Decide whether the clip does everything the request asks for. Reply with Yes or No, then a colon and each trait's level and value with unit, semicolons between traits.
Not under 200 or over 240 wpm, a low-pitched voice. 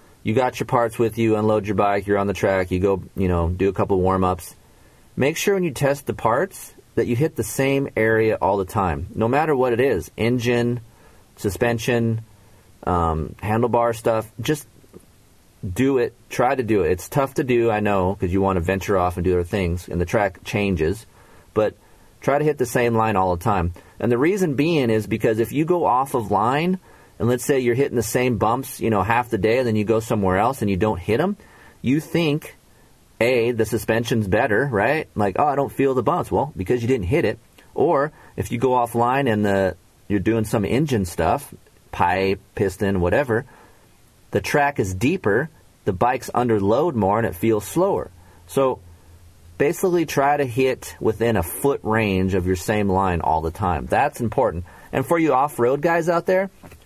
Yes: fast, 205 wpm; low, 110 Hz